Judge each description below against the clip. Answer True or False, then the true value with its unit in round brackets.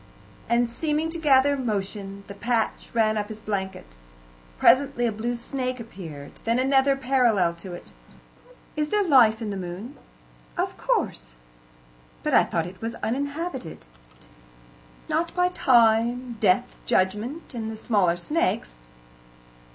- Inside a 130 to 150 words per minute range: True (135 wpm)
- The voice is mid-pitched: False (230 Hz)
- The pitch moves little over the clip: False (5.1 semitones)